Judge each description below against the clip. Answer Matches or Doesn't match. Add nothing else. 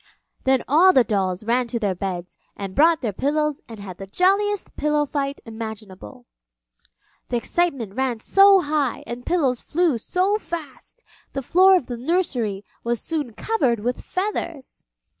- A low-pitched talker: Doesn't match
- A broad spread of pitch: Matches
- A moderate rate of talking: Matches